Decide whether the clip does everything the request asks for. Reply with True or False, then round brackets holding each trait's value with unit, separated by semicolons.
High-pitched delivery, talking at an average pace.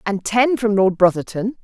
True (210 Hz; 185 wpm)